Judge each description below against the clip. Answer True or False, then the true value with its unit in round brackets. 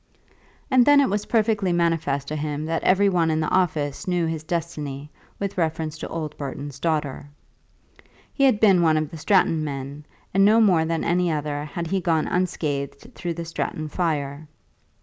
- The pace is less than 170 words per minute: False (180 wpm)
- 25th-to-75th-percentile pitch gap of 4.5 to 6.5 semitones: False (3.4 semitones)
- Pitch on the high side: False (160 Hz)